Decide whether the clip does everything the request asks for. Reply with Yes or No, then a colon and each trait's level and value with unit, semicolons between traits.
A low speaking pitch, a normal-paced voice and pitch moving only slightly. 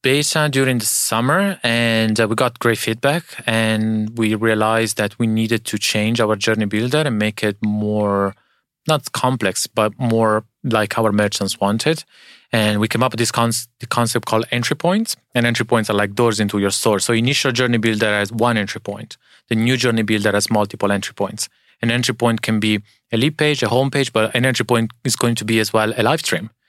No: low, 115 Hz; fast, 215 wpm; narrow, 2.2 semitones